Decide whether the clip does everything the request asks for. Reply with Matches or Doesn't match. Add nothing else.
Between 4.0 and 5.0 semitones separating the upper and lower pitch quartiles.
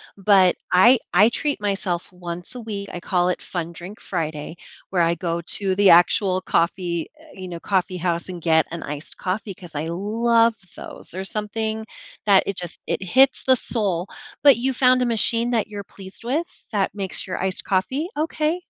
Matches